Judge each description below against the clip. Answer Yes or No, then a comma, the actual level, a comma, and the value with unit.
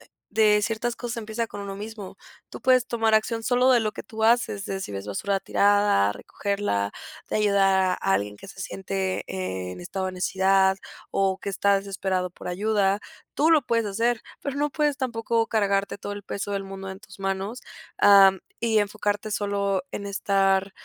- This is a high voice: Yes, high, 200 Hz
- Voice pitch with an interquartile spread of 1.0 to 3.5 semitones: Yes, narrow, 2.5 semitones